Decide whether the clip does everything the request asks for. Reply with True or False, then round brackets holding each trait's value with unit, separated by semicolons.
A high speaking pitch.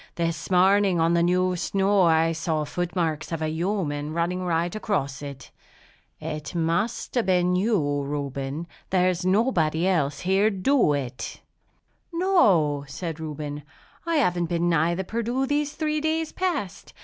False (175 Hz)